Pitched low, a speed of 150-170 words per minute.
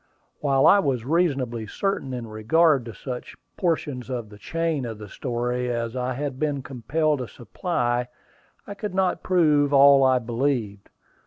Yes: low, 130 Hz; average, 160 wpm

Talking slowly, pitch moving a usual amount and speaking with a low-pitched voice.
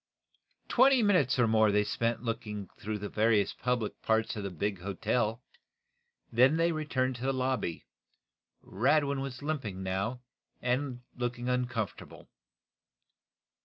Yes: slow, 130 wpm; average, 3.8 semitones; low, 120 Hz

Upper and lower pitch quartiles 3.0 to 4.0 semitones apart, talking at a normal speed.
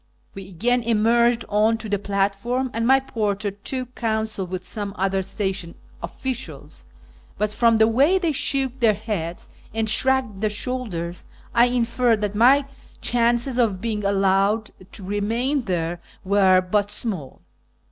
Yes: average, 3.5 semitones; average, 145 wpm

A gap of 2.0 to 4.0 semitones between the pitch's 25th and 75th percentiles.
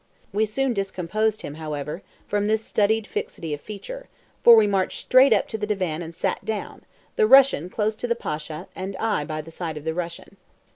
No: average, 5.1 semitones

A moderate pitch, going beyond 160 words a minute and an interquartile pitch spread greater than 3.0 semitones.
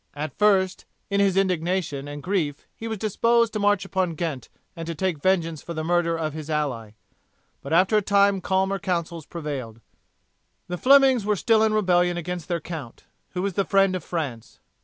Yes: medium, 180 Hz; average, 185 wpm; average, 3.9 semitones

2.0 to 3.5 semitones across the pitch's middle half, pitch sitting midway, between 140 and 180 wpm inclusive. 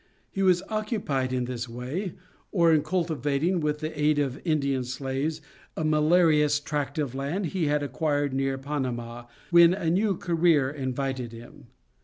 No: average, 4.0 semitones; medium, 150 Hz; average, 155 wpm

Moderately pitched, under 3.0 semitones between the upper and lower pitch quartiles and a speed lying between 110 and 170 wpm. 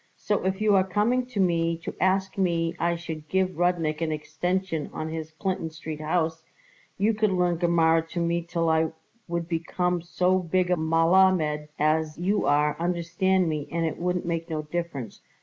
No: medium, 170 Hz; narrow, 2.5 semitones; average, 180 wpm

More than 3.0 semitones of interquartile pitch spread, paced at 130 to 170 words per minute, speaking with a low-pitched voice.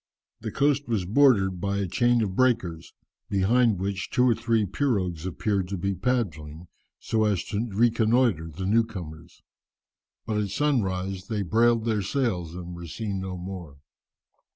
Yes: average, 4.2 semitones; average, 155 wpm; low, 100 Hz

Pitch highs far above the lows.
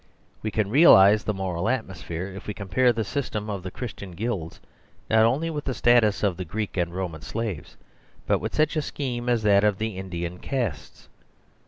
No: average, 4.2 semitones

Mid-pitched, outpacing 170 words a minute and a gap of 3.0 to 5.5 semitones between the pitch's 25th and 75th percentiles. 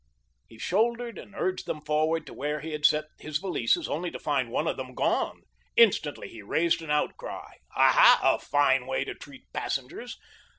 Yes: medium, 150 Hz; average, 180 wpm; average, 3.9 semitones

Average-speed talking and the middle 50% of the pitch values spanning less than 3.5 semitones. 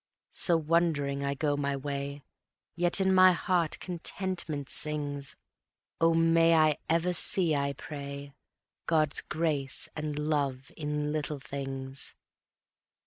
No: slow, 120 wpm; average, 2.9 semitones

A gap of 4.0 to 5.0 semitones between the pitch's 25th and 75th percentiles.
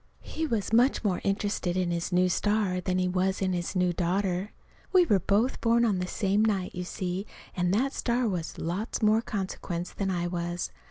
No: average, 3.1 semitones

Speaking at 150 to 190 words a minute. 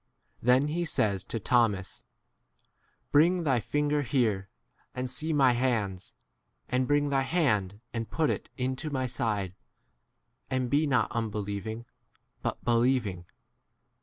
No: slow, 135 wpm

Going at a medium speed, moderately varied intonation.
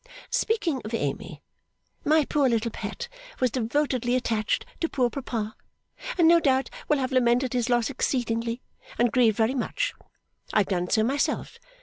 Yes: average, 155 wpm; average, 3.4 semitones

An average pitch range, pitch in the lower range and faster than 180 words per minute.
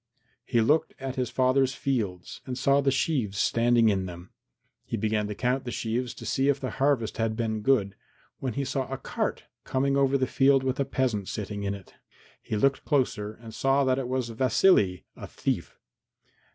Yes: average, 3.7 semitones; low, 125 Hz; average, 190 wpm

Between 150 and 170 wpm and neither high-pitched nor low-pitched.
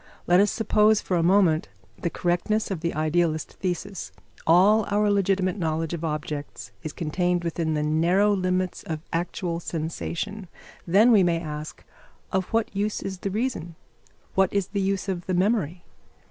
Yes: average, 160 wpm; medium, 180 Hz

